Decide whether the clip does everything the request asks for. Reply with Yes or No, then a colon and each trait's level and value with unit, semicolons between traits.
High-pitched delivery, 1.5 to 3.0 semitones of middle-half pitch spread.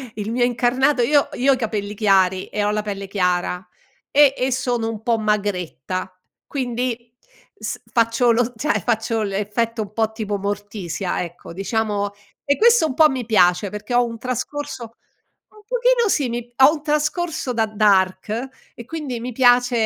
No: high, 230 Hz; average, 3.7 semitones